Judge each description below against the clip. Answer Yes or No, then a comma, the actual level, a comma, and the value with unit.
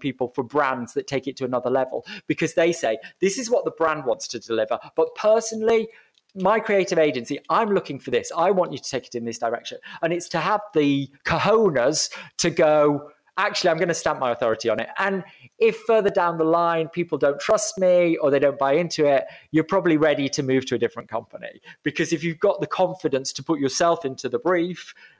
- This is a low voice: No, medium, 160 Hz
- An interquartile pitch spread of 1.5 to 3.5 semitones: No, average, 5.0 semitones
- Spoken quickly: Yes, fast, 220 wpm